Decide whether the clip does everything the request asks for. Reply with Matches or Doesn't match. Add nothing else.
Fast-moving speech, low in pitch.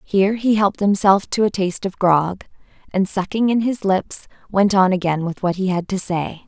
Doesn't match